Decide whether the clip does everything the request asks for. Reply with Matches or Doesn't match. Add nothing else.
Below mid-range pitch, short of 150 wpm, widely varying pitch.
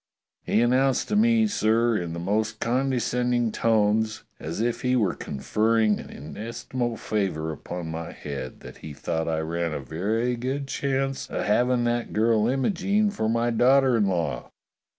Doesn't match